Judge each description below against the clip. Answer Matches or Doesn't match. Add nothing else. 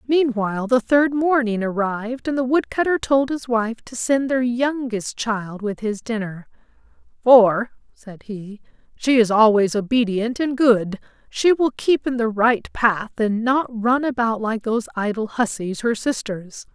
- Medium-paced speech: Matches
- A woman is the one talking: Matches